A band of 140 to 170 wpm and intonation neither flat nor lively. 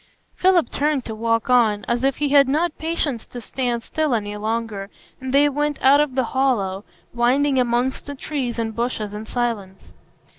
No: average, 180 wpm; average, 3.8 semitones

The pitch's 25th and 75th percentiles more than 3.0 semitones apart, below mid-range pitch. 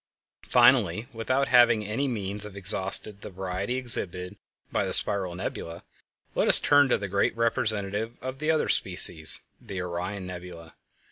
Yes: average, 4.3 semitones; low, 100 Hz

